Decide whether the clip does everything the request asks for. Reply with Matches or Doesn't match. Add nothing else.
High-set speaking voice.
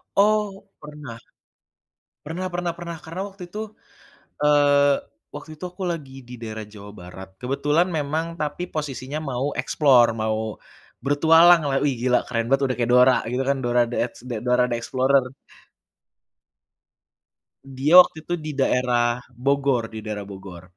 Doesn't match